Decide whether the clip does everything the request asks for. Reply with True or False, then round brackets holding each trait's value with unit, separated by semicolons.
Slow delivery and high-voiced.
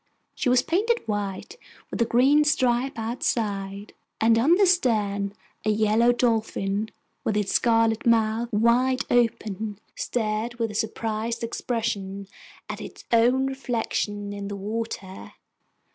True (130 wpm; 225 Hz)